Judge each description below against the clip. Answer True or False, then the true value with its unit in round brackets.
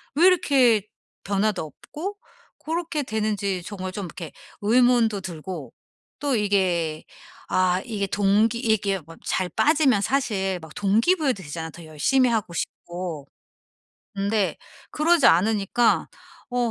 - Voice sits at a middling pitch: False (205 Hz)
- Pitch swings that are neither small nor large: True (4.9 semitones)